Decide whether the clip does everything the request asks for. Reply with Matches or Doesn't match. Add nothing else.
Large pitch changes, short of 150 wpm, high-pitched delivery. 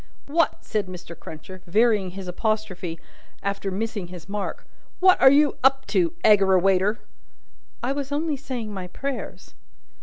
Matches